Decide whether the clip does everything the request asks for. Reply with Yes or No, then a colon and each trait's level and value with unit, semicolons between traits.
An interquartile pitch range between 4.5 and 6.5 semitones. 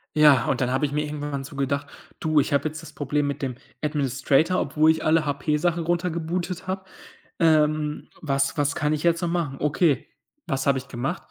No: narrow, 2.6 semitones